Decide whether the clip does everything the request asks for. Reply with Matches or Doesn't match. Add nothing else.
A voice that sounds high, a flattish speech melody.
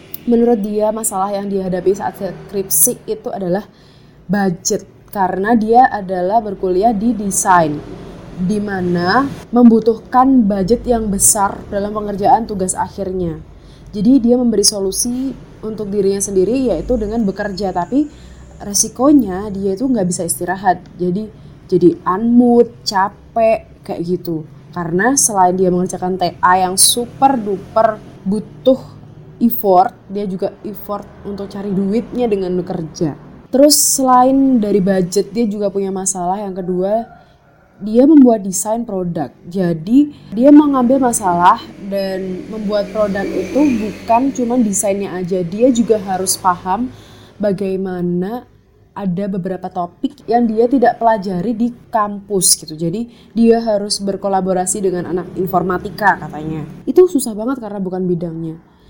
Doesn't match